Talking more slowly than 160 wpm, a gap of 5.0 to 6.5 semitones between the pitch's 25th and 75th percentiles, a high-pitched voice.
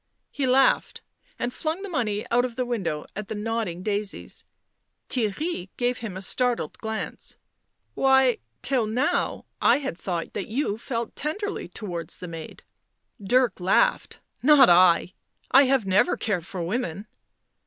Yes: average, 150 wpm; average, 5.3 semitones; high, 225 Hz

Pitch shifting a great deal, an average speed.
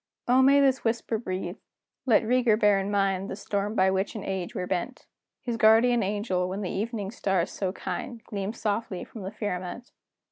No: average, 3.2 semitones; average, 185 wpm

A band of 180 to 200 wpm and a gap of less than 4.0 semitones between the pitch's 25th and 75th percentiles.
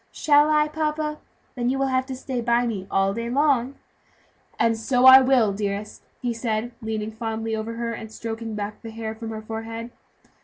Yes: average, 190 wpm; average, 2.9 semitones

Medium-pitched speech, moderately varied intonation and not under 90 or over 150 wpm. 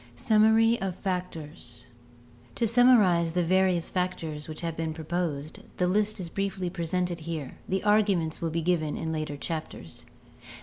Yes: medium, 175 Hz; average, 3.2 semitones; average, 145 wpm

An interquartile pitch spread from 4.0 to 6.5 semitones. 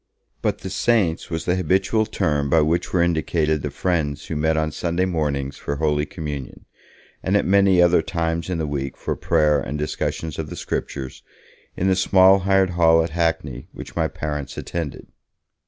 No: average, 3.5 semitones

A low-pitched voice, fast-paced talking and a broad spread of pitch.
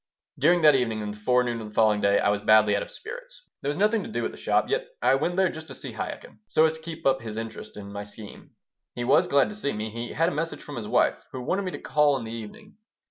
Yes: low, 130 Hz; fast, 290 wpm; wide, 7.2 semitones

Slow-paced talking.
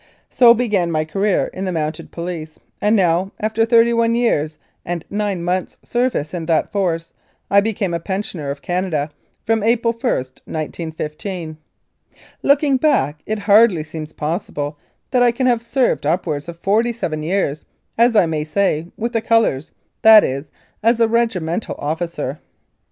No: average, 155 wpm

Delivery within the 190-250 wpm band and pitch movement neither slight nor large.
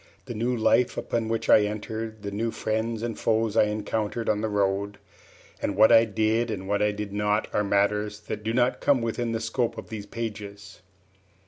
No: average, 200 wpm; narrow, 1.7 semitones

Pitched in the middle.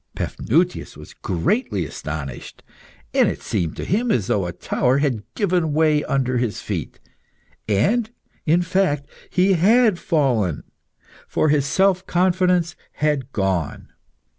Yes: medium, 150 Hz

